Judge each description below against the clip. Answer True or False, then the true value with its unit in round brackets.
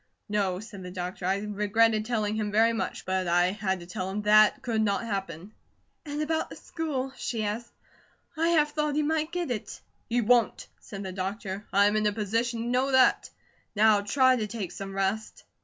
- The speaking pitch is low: False (215 Hz)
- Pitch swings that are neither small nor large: True (3.7 semitones)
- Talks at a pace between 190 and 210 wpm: True (195 wpm)